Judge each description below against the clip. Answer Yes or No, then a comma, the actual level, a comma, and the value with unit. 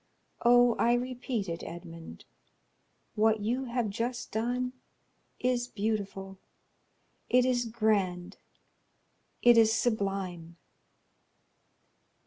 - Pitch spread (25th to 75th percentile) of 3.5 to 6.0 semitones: Yes, average, 3.8 semitones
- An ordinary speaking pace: No, slow, 85 wpm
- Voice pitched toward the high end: Yes, high, 220 Hz